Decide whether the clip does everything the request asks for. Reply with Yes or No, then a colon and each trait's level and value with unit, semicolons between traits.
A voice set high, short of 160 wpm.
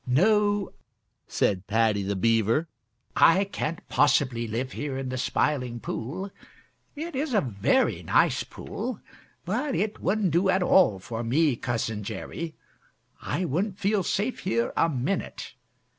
No: medium, 150 Hz; average, 140 wpm